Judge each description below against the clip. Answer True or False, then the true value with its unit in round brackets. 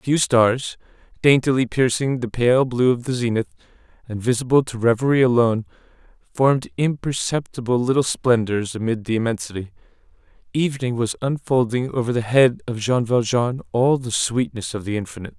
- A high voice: False (120 Hz)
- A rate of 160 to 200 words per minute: False (150 wpm)